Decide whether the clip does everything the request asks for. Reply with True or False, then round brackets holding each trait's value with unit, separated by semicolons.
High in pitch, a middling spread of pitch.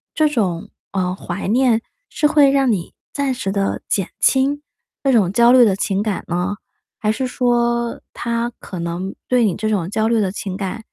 True (220 Hz; 4.3 semitones)